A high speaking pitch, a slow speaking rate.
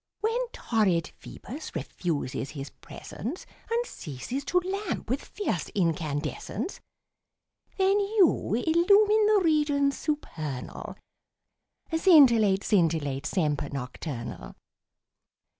Yes: high, 240 Hz; slow, 90 wpm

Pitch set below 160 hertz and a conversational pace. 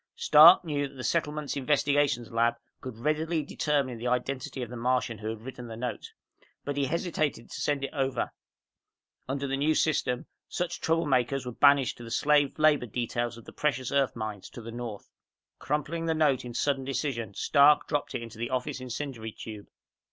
Yes: low, 135 Hz; average, 190 wpm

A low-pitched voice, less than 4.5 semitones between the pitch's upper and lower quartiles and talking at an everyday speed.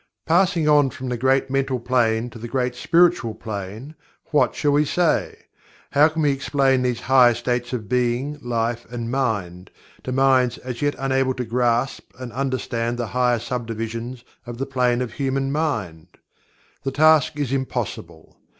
Yes: low, 125 Hz; narrow, 2.4 semitones; average, 160 wpm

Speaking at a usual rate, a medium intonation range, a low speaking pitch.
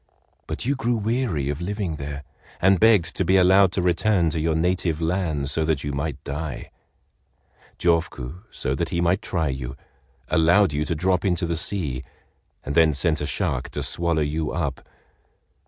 Yes: average, 175 wpm; average, 3.9 semitones; very low, 85 Hz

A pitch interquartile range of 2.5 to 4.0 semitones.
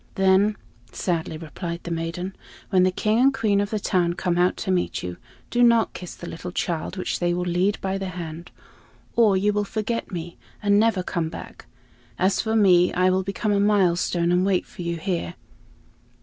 Yes: average, 2.8 semitones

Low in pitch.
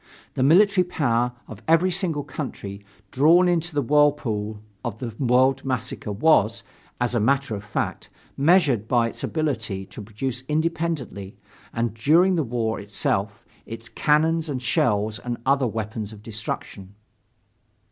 Yes: low, 125 Hz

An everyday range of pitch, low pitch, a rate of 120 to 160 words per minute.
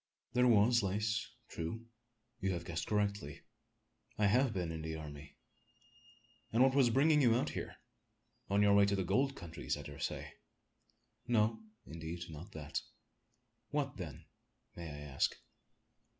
No: wide, 6.0 semitones; low, 100 Hz; average, 150 wpm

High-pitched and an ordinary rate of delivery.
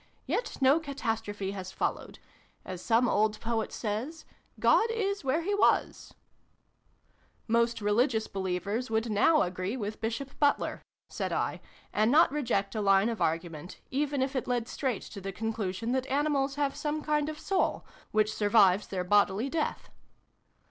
Yes: high, 230 Hz; average, 160 wpm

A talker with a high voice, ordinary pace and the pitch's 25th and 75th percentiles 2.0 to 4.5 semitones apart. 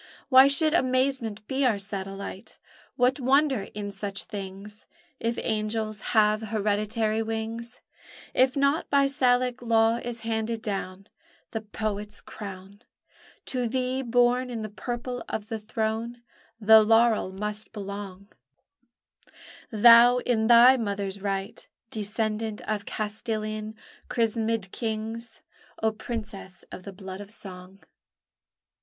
No: high, 220 Hz; slow, 120 wpm; average, 2.7 semitones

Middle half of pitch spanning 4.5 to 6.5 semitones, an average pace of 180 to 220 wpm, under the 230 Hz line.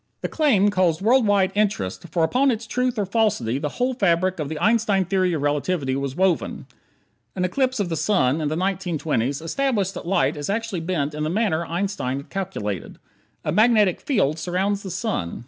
Yes: average, 5.2 semitones; average, 190 wpm; medium, 185 Hz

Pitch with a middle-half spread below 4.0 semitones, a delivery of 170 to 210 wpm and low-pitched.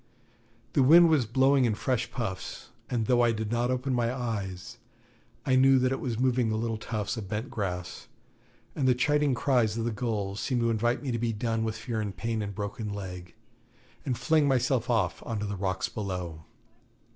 Yes: average, 3.5 semitones; average, 200 wpm; low, 115 Hz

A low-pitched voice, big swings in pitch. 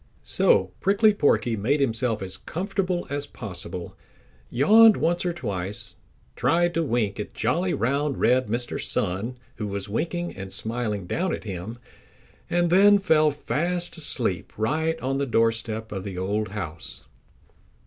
Yes: low, 125 Hz; wide, 8.3 semitones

